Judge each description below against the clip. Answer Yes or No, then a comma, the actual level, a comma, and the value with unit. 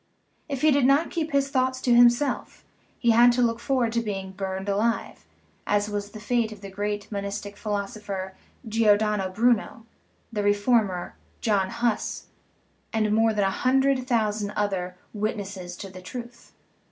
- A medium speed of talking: Yes, average, 160 wpm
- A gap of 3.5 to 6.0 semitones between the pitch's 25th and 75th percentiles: No, average, 3.0 semitones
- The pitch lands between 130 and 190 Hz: No, high, 215 Hz